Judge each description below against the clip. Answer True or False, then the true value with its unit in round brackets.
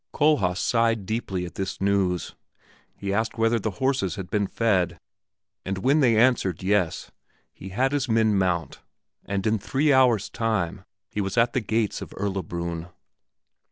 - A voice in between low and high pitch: False (105 Hz)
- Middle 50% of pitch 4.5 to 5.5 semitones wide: False (3.7 semitones)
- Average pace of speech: True (160 wpm)